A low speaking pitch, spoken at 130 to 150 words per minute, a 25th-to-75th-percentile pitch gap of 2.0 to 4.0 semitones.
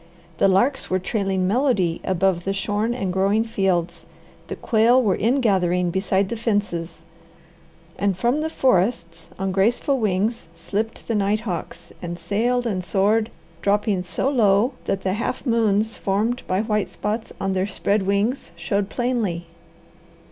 No: high, 200 Hz; average, 145 wpm; average, 3.3 semitones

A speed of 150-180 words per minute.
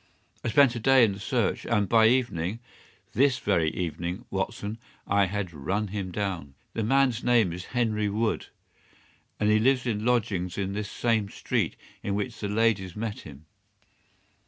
Yes: average, 160 wpm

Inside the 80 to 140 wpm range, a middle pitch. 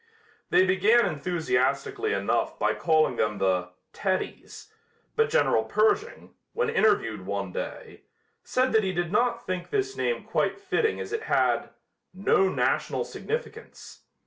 No: slow, 135 wpm; high, 195 Hz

